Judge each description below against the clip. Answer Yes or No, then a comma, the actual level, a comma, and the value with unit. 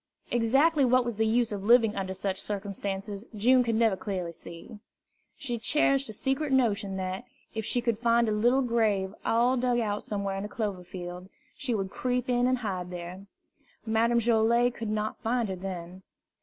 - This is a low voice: No, high, 220 Hz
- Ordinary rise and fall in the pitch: Yes, average, 3.8 semitones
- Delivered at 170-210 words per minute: Yes, average, 185 wpm